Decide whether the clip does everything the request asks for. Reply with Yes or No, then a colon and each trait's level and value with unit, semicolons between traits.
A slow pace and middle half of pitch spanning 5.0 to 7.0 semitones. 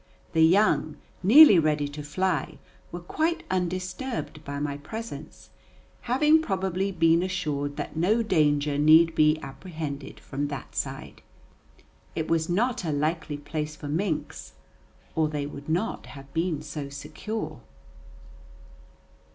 No: slow, 125 wpm; average, 4.1 semitones